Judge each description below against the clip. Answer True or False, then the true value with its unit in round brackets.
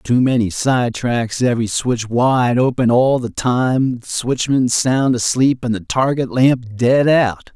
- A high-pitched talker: False (125 Hz)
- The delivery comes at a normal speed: True (160 wpm)